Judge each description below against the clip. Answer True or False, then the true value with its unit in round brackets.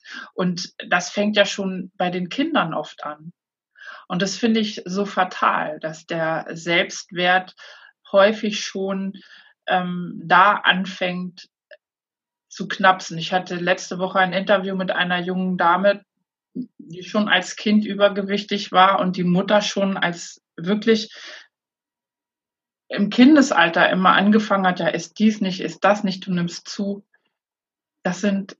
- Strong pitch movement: False (2.4 semitones)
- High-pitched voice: True (195 Hz)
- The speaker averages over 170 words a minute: False (135 wpm)